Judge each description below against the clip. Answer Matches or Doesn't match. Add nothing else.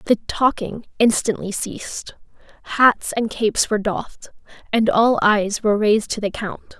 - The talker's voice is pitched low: Doesn't match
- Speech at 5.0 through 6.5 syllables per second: Doesn't match